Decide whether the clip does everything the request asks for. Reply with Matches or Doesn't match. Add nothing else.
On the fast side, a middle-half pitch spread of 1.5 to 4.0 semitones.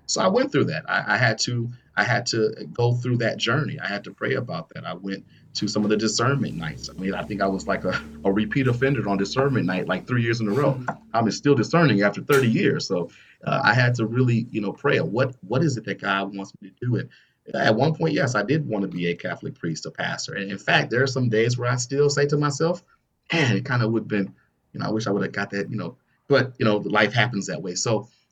Doesn't match